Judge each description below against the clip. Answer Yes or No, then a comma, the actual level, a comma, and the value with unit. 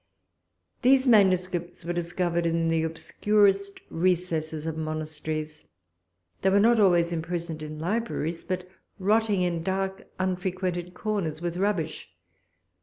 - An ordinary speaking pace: No, slow, 115 wpm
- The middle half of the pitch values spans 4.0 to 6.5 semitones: No, average, 2.9 semitones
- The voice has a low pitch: No, medium, 175 Hz